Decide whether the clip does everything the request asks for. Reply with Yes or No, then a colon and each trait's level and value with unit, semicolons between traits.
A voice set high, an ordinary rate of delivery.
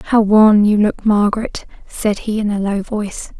Yes: high, 210 Hz; average, 195 wpm